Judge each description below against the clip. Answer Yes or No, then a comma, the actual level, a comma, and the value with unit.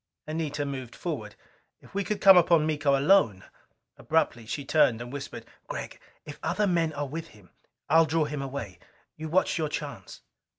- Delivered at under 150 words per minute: No, average, 170 wpm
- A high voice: No, medium, 150 Hz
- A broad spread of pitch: No, average, 3.2 semitones